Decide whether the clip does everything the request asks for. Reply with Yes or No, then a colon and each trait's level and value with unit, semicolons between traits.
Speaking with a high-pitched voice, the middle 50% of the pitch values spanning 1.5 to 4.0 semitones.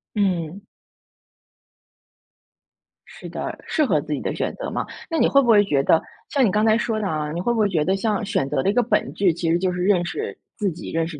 No: high, 195 Hz; average, 4.8 semitones